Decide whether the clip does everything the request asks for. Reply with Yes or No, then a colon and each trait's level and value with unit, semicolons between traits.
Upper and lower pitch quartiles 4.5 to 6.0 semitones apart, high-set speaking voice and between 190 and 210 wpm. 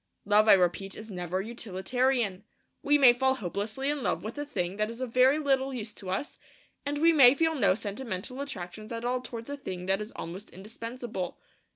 Yes: wide, 5.4 semitones; high, 230 Hz; average, 200 wpm